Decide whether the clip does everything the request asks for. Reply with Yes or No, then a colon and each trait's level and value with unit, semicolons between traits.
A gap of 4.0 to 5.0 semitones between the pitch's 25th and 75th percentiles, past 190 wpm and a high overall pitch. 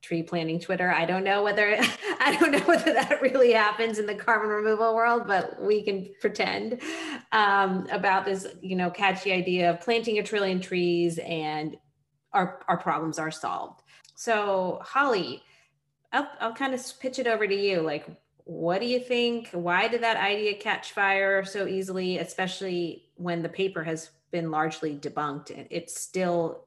No: average, 4.4 semitones; average, 170 wpm; high, 195 Hz